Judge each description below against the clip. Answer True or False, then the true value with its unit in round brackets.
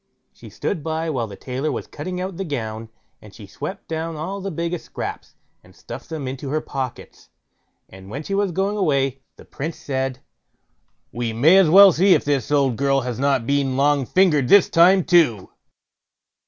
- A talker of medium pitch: True (145 Hz)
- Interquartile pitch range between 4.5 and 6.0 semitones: True (4.8 semitones)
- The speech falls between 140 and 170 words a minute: False (185 wpm)